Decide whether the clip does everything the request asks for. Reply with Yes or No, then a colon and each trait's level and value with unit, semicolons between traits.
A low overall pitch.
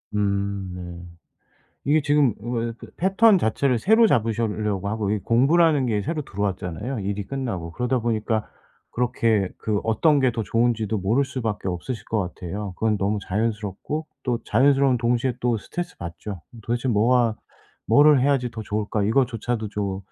Yes: low, 115 Hz